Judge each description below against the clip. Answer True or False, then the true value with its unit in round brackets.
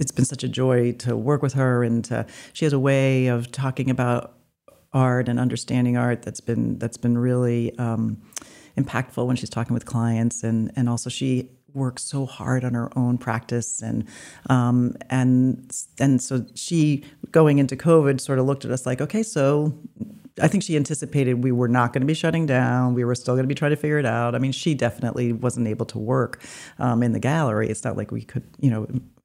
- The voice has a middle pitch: False (125 Hz)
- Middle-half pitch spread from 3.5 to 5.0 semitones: False (2.4 semitones)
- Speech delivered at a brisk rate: True (215 wpm)